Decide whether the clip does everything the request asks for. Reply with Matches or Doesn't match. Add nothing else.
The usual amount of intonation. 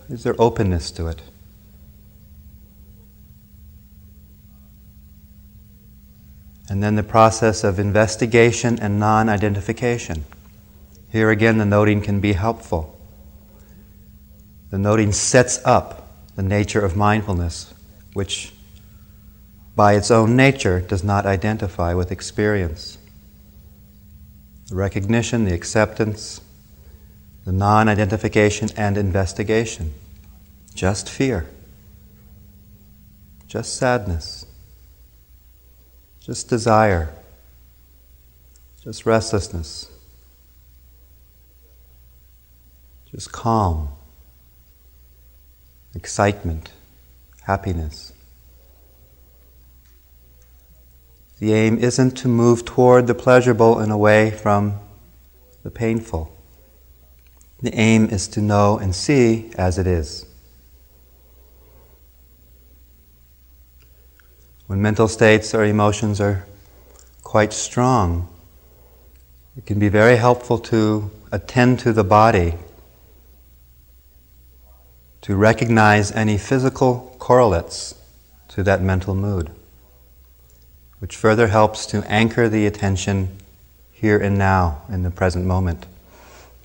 Doesn't match